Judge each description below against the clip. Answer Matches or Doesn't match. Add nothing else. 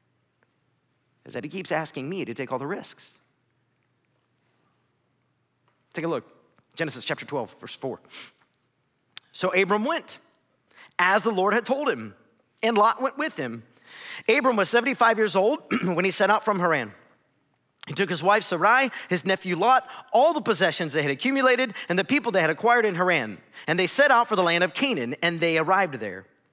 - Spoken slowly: Doesn't match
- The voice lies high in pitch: Matches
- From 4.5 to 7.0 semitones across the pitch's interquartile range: Matches